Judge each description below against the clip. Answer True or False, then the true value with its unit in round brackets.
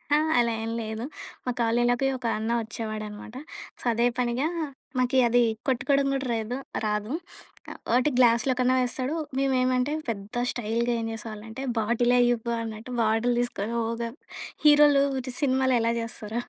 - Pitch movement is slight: True (2.2 semitones)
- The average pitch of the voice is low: False (240 Hz)